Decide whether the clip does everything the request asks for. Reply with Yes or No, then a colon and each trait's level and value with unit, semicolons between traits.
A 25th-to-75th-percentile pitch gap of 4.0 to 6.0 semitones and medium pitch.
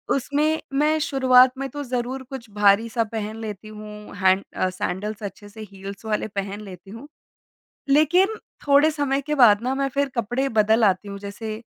No: average, 4.9 semitones; high, 225 Hz